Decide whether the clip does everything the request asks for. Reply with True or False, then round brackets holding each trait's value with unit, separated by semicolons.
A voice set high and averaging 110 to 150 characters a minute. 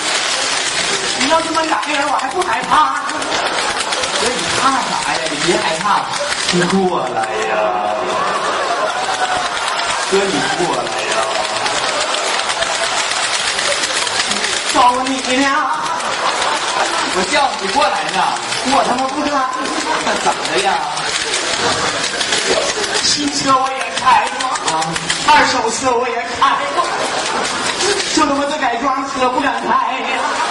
True (260 Hz; 140 characters per minute)